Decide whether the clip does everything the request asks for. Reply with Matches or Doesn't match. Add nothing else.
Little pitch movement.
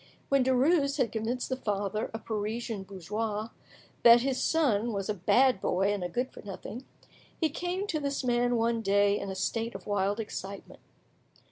Doesn't match